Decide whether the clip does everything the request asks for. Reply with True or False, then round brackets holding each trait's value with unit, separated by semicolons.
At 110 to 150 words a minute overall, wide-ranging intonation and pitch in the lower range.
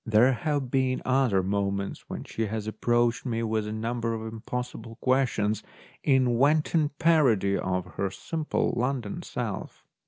False (145 wpm; 3.5 semitones; 120 Hz)